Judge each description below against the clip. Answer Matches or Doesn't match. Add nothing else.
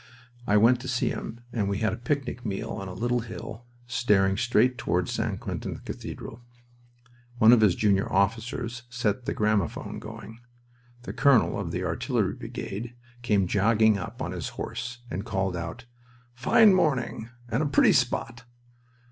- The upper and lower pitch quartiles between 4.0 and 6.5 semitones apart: Doesn't match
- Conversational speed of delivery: Matches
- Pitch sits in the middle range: Doesn't match